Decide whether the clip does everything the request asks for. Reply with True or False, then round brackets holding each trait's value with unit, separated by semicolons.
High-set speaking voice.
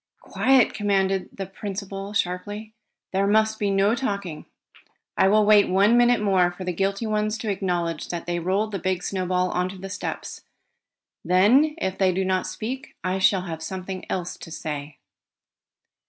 True (195 Hz)